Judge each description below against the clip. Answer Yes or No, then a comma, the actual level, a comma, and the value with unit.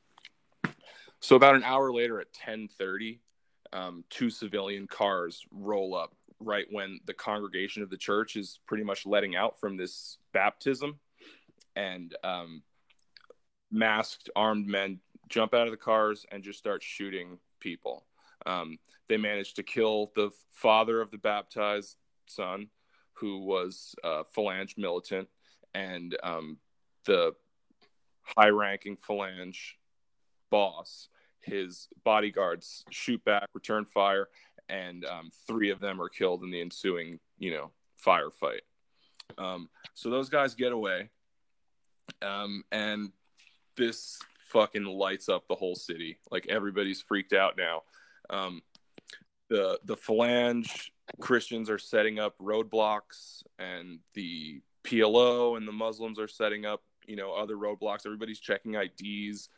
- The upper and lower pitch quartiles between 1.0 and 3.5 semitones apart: Yes, narrow, 2.4 semitones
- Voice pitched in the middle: No, low, 105 Hz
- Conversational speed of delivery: No, slow, 130 wpm